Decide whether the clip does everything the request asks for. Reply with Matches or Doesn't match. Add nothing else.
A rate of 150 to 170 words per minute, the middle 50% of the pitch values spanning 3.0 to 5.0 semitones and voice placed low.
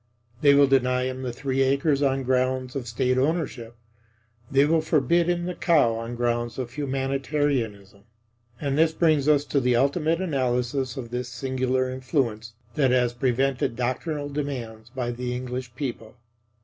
Doesn't match